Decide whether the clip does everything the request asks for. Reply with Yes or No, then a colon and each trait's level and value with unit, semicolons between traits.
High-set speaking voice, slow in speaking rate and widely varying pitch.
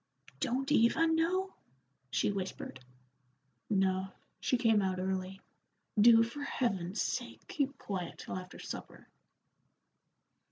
Yes: high, 215 Hz; slow, 110 wpm; wide, 6.3 semitones